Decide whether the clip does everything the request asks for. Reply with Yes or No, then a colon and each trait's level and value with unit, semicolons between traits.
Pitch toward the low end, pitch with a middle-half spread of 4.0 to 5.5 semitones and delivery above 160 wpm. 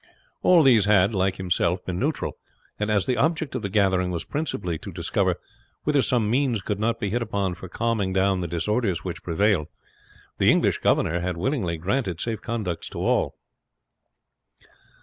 Yes: low, 100 Hz; average, 4.3 semitones; average, 170 wpm